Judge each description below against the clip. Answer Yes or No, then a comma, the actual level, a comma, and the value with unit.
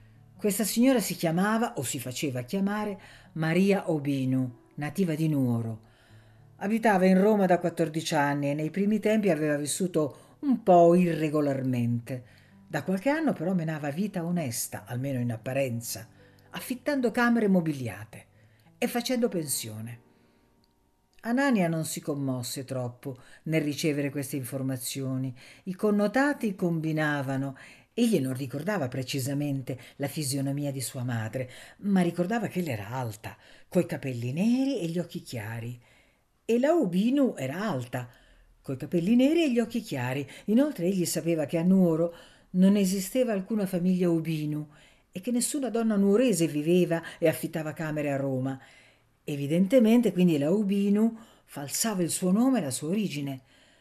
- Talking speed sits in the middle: Yes, average, 140 wpm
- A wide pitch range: Yes, wide, 6.7 semitones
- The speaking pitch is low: No, medium, 160 Hz